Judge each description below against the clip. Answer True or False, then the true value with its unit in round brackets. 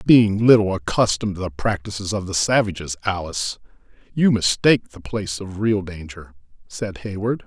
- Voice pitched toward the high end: False (100 Hz)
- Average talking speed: True (155 wpm)